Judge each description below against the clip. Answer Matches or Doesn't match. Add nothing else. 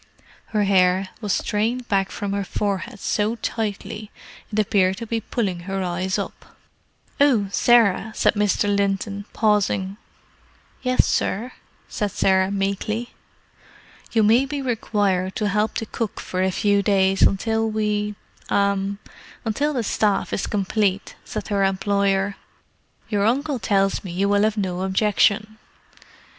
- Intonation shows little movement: Matches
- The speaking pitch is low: Doesn't match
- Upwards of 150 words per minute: Doesn't match